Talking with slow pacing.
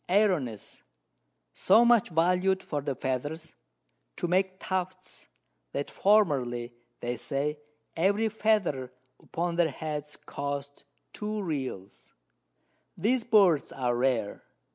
Yes: slow, 105 wpm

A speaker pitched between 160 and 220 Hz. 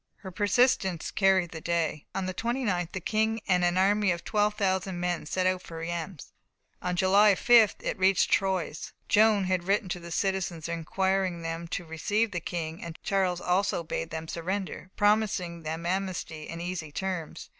Yes: medium, 185 Hz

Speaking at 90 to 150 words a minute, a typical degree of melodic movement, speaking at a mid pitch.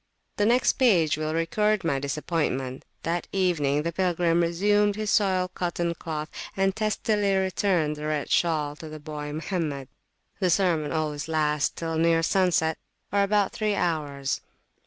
Yes: average, 145 wpm; average, 4.1 semitones; medium, 165 Hz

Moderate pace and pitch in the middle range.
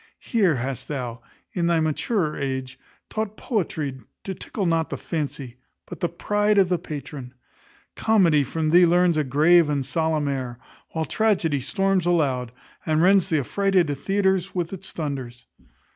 Yes: average, 155 wpm; medium, 160 Hz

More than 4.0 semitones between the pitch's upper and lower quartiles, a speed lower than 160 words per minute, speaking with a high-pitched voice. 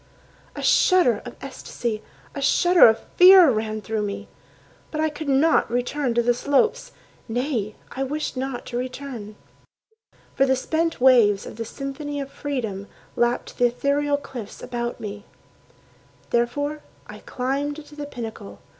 No: average, 3.7 semitones; average, 145 wpm; very high, 260 Hz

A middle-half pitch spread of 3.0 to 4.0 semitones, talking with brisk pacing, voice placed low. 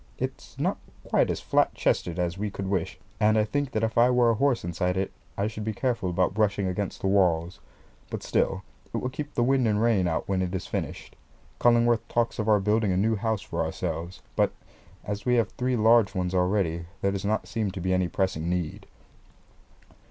Yes: average, 3.6 semitones; fast, 210 wpm; low, 100 Hz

